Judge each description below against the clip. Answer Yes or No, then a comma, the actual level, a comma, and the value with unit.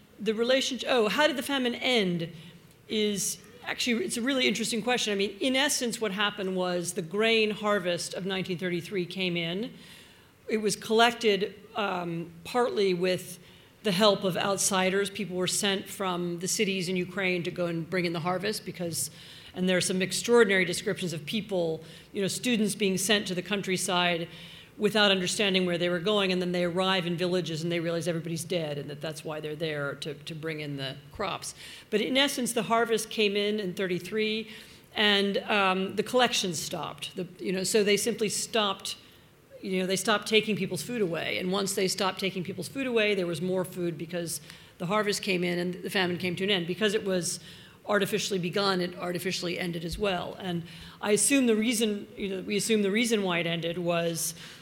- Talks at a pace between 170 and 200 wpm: Yes, average, 195 wpm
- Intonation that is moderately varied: Yes, average, 3.2 semitones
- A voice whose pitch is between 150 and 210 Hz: Yes, high, 190 Hz